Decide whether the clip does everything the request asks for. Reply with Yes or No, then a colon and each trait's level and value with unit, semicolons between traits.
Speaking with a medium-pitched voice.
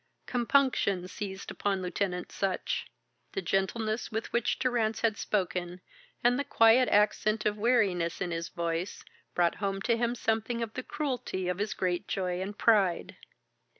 No: high, 210 Hz